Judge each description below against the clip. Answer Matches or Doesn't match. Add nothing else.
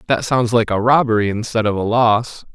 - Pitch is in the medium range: Doesn't match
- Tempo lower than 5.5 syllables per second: Matches